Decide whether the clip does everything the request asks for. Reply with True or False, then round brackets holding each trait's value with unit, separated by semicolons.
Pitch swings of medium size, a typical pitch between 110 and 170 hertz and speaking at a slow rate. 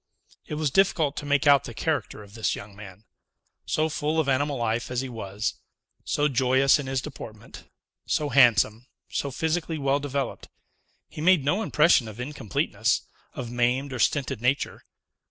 False (3.7 semitones; 135 Hz; 165 wpm)